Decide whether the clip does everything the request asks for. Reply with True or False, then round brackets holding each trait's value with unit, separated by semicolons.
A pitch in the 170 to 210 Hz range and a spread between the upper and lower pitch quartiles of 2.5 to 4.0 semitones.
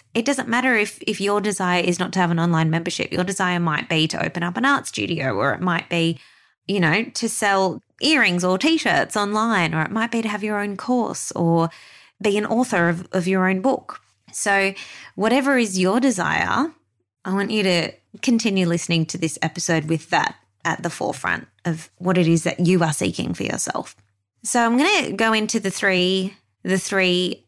False (190 Hz; 4.6 semitones)